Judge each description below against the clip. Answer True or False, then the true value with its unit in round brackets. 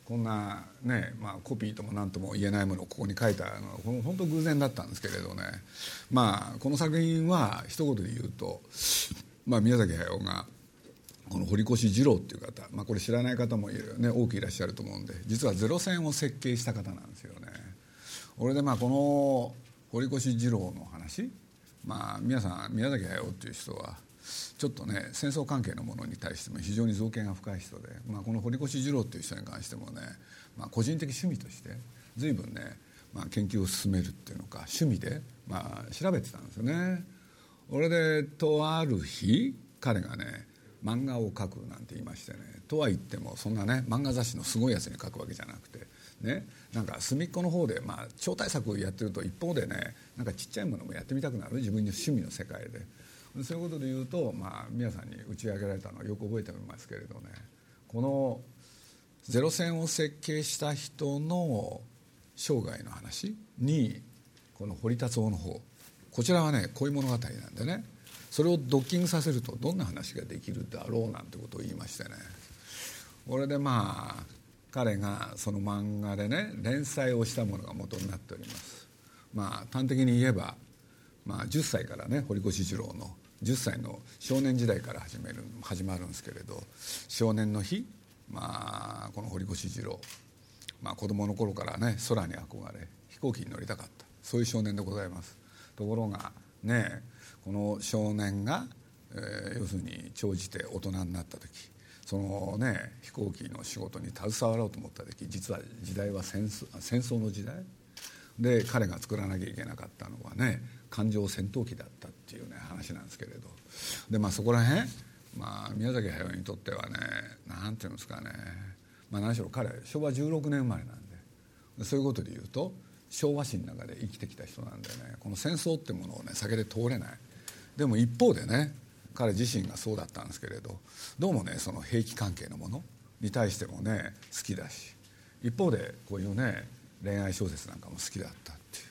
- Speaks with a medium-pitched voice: False (115 Hz)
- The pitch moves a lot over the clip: False (3.8 semitones)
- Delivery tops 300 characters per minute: True (345 characters per minute)